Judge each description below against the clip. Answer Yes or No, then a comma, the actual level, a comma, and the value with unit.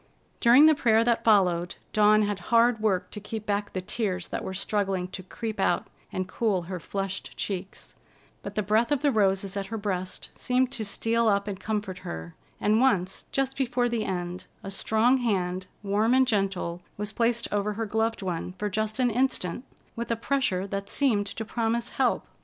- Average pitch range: Yes, average, 3.4 semitones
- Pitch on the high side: Yes, high, 210 Hz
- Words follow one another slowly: No, average, 190 wpm